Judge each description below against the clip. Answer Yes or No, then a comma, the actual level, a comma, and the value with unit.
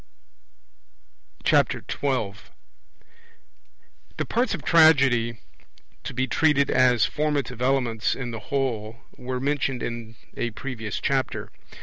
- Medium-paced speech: No, slow, 100 wpm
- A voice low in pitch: Yes, low, 130 Hz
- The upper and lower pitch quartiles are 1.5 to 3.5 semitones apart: Yes, average, 3.1 semitones